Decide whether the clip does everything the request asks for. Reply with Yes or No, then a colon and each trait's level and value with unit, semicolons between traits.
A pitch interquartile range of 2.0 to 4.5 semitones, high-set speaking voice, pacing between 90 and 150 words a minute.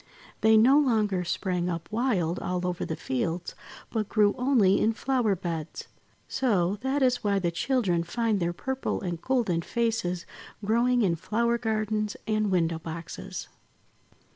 No: average, 5.1 semitones; high, 205 Hz; average, 145 wpm